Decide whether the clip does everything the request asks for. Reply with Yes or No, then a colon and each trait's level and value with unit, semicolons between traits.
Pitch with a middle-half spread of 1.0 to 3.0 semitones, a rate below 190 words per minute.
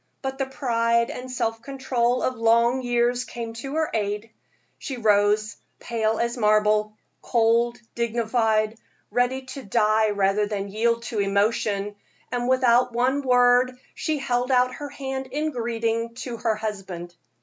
Yes: average, 2.7 semitones; average, 145 wpm